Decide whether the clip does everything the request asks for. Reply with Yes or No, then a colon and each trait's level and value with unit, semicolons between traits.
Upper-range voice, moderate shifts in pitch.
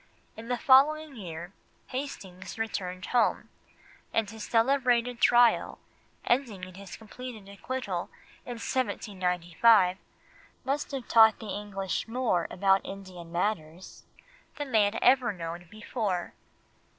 Yes: high, 215 Hz; average, 5.0 semitones